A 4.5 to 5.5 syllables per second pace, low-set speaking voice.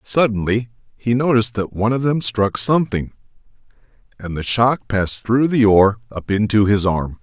Yes: 5.1 syllables/s; low, 110 Hz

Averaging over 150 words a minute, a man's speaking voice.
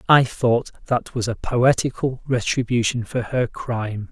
No: average, 145 wpm; male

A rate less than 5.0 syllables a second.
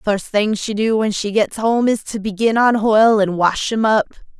Yes: 4.7 syllables/s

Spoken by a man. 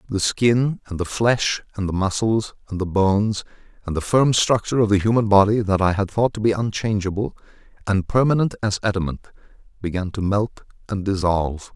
Yes: male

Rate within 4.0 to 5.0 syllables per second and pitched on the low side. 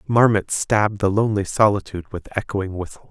No: 5.7 syllables/s; low, 100 Hz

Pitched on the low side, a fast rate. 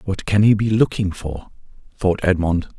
No: very low, 95 Hz; average, 170 wpm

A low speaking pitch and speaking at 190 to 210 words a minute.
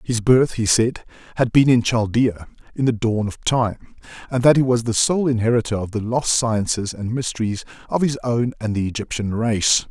Yes: low, 115 Hz; average, 200 wpm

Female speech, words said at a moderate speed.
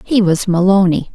Yes: female; average, 155 wpm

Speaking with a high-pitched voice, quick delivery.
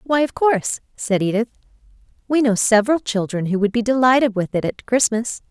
No: high, 225 Hz; average, 185 wpm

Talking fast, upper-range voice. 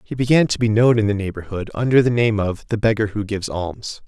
No: fast, 250 wpm; low, 110 Hz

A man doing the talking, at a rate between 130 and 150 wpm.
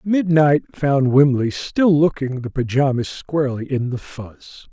Yes: male; average, 140 wpm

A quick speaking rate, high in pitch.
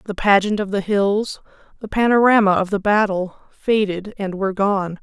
No: average, 165 wpm; high, 200 Hz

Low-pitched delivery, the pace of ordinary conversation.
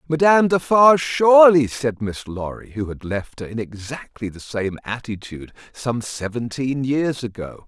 Yes: low, 125 Hz; average, 150 wpm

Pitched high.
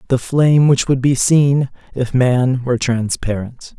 No: low, 130 Hz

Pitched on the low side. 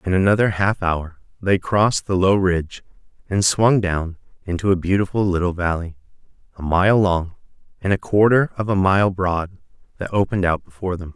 Yes: very low, 95 Hz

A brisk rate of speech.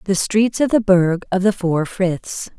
Yes: fast, 210 wpm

